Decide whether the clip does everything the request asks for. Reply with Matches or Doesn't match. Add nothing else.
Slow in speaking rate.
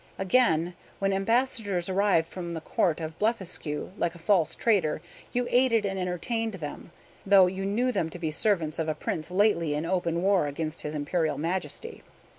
Doesn't match